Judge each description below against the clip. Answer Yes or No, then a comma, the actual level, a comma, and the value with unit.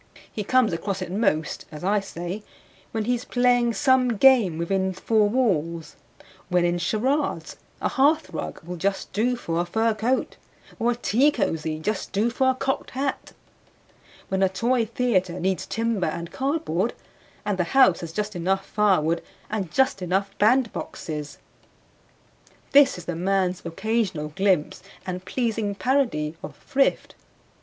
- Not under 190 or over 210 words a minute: No, average, 150 wpm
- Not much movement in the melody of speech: No, wide, 5.5 semitones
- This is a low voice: No, high, 200 Hz